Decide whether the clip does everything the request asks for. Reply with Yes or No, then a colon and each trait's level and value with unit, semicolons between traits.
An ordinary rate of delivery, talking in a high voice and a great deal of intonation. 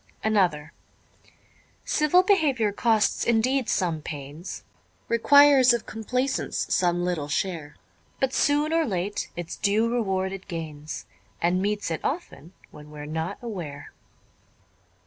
No: slow, 125 wpm; high, 200 Hz; wide, 6.8 semitones